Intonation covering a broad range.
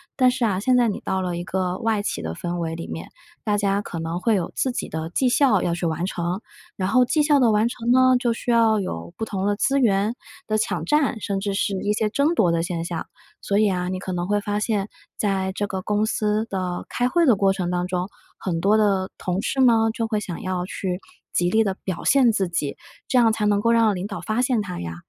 No: average, 3.9 semitones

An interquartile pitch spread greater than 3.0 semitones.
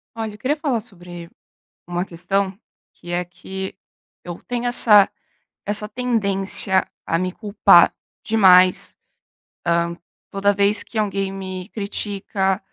No: narrow, 2.5 semitones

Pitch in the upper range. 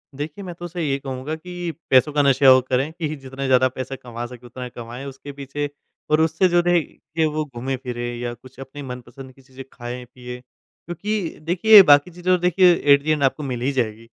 No: low, 135 Hz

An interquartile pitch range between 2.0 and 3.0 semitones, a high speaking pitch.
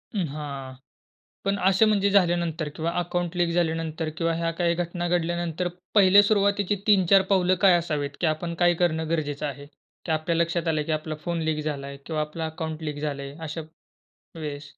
No: narrow, 2.4 semitones; medium, 165 Hz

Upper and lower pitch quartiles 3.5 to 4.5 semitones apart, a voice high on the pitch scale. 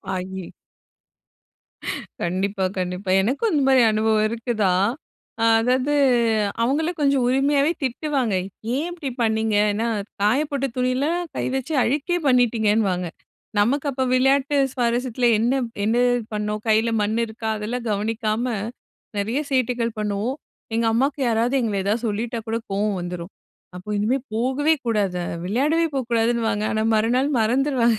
Yes: average, 3.8 semitones; high, 230 Hz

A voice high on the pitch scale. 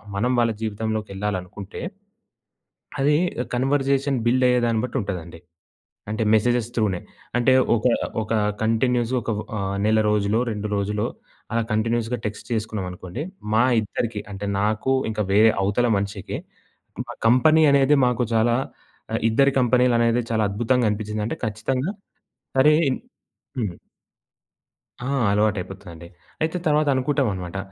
No: low, 110 Hz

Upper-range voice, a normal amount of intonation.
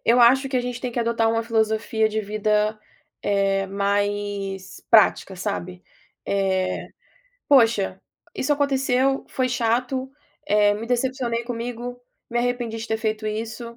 Yes: high, 225 Hz; average, 3.1 semitones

